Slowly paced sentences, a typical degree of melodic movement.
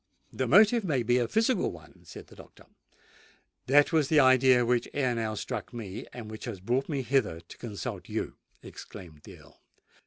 No: average, 185 wpm; average, 4.4 semitones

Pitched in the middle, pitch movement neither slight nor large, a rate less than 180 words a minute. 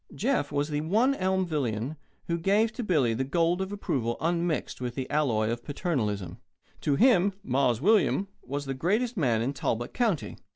No: medium, 150 Hz; wide, 7.1 semitones; average, 170 wpm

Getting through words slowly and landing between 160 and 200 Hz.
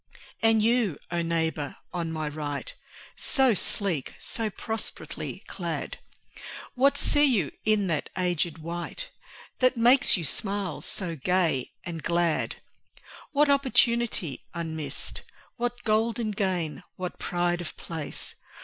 Yes: slow, 120 wpm; medium, 185 Hz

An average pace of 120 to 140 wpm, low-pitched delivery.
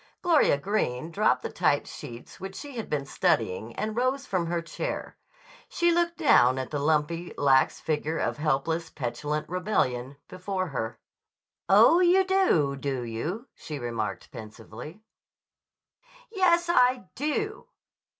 No: slow, 135 wpm; medium, 170 Hz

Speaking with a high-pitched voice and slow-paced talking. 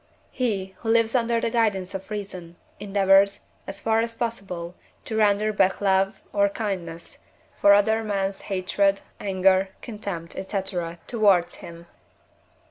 Yes: high, 200 Hz; slow, 130 wpm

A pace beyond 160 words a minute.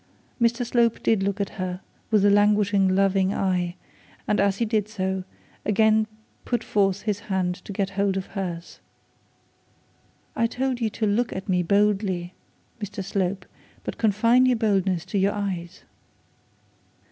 No: average, 155 wpm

